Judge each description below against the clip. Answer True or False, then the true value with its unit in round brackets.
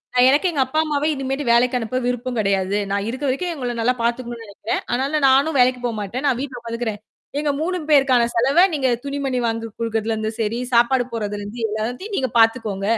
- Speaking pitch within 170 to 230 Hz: False (245 Hz)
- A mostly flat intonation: False (3.2 semitones)